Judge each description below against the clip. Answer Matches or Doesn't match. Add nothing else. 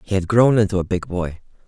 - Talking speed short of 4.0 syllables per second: Doesn't match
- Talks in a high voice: Doesn't match